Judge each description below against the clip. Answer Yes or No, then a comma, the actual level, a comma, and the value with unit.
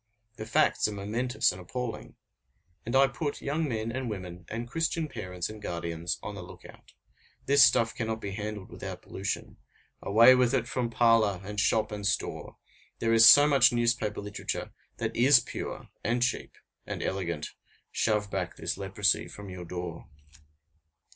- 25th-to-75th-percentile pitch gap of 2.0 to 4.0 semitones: Yes, average, 3.7 semitones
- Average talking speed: Yes, average, 165 wpm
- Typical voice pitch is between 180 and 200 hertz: No, low, 110 Hz